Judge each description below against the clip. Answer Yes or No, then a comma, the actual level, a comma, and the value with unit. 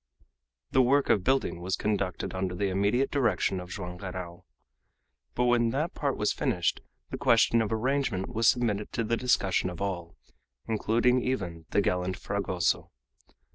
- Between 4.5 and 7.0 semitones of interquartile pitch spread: Yes, average, 4.8 semitones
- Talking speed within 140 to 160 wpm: Yes, average, 155 wpm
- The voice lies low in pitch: Yes, low, 100 Hz